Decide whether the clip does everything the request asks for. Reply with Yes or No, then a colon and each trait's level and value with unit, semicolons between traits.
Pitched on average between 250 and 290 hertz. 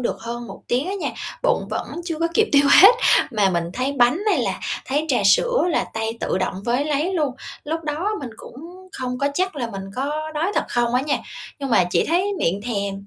Yes: very high, 275 Hz